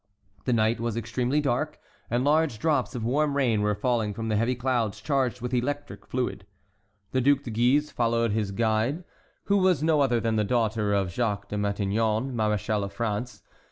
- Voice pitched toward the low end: Yes, low, 120 Hz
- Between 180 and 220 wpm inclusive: Yes, average, 185 wpm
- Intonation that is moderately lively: Yes, average, 3.6 semitones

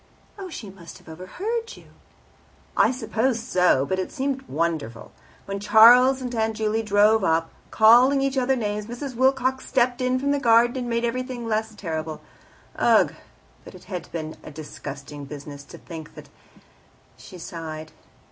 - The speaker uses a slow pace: No, average, 165 wpm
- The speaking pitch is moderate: No, high, 220 Hz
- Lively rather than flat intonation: Yes, wide, 7.4 semitones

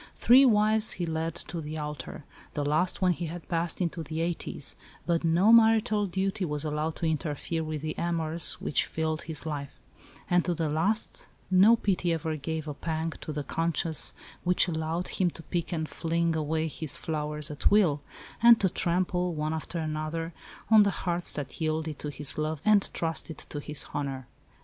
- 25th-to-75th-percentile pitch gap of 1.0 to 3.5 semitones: Yes, narrow, 2.4 semitones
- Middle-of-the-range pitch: Yes, medium, 165 Hz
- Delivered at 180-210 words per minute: Yes, average, 185 wpm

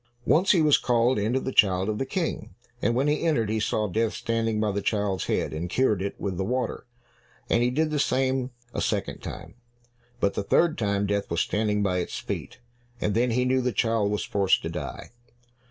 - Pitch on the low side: Yes, low, 110 Hz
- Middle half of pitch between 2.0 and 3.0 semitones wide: No, average, 4.1 semitones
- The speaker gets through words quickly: Yes, fast, 220 wpm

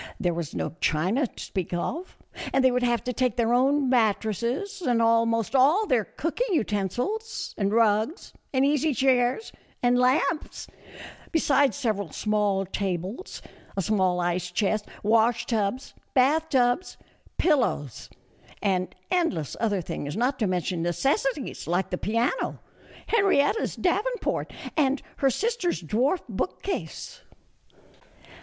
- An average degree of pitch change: No, wide, 6.0 semitones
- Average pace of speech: No, slow, 125 wpm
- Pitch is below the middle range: No, high, 240 Hz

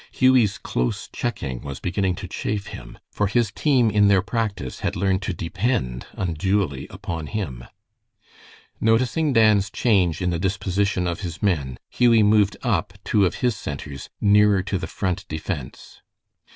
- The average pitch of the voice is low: Yes, very low, 95 Hz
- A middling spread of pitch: Yes, average, 4.0 semitones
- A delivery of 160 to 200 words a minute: No, average, 150 wpm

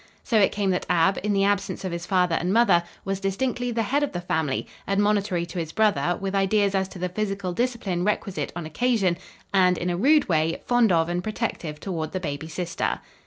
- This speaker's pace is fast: Yes, fast, 215 wpm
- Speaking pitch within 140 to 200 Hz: Yes, high, 190 Hz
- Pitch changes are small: No, average, 3.2 semitones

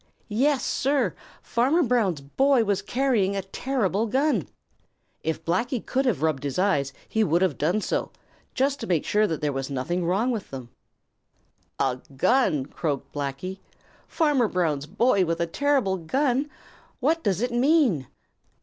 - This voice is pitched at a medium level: No, high, 200 Hz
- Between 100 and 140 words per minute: No, average, 160 wpm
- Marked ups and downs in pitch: Yes, wide, 8.1 semitones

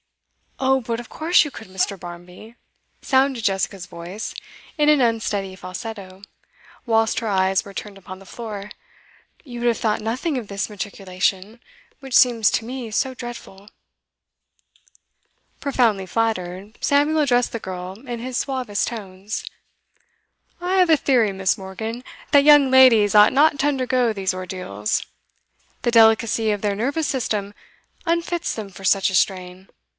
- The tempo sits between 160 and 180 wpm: No, average, 150 wpm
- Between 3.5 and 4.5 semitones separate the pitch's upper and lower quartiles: No, average, 4.9 semitones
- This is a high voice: Yes, high, 220 Hz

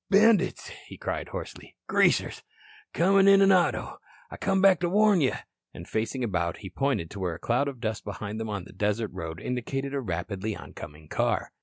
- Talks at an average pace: Yes, average, 190 wpm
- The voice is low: Yes, low, 115 Hz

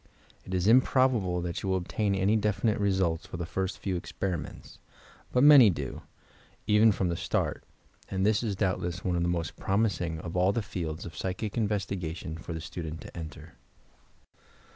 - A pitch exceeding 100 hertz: No, very low, 95 Hz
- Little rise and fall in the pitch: No, average, 3.4 semitones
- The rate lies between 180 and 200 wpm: Yes, average, 185 wpm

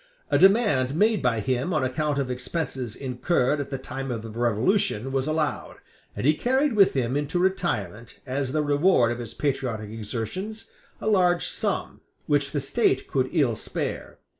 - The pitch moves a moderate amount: No, wide, 5.8 semitones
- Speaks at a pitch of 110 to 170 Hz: Yes, low, 135 Hz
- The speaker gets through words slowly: No, average, 170 wpm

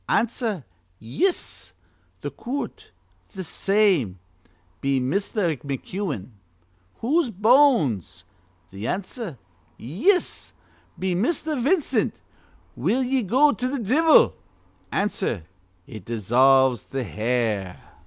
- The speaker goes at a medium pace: No, slow, 90 wpm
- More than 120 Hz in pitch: Yes, high, 190 Hz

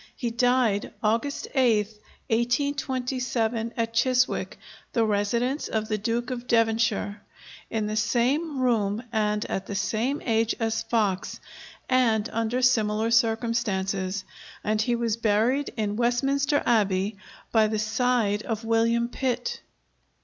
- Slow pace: Yes, slow, 125 wpm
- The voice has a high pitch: Yes, high, 230 Hz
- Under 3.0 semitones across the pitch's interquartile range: Yes, narrow, 2.5 semitones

